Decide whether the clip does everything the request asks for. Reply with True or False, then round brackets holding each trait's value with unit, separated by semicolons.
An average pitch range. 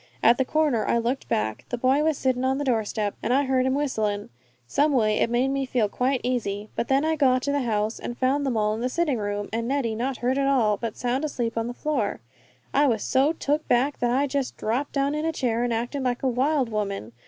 True (3.4 semitones)